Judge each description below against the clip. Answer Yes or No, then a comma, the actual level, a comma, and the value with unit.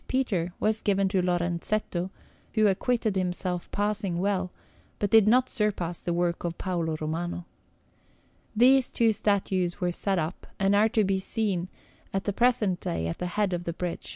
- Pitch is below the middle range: No, high, 190 Hz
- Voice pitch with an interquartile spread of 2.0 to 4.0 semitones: Yes, average, 3.3 semitones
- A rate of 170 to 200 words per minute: Yes, average, 180 wpm